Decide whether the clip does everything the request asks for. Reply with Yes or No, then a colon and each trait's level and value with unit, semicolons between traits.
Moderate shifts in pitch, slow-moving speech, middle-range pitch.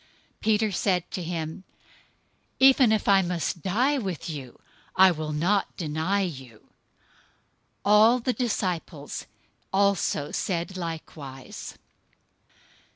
Yes: average, 4.6 semitones; slow, 110 wpm; medium, 180 Hz